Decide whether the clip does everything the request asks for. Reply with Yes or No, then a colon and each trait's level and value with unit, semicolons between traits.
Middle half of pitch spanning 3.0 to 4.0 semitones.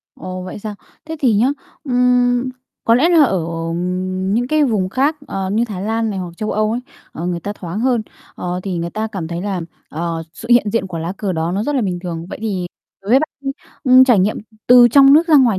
No: average, 5.2 semitones